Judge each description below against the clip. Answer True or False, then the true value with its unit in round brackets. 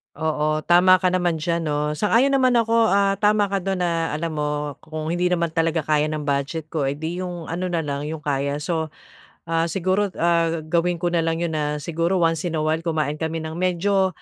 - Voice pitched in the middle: True (165 Hz)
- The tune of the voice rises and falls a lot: False (2.6 semitones)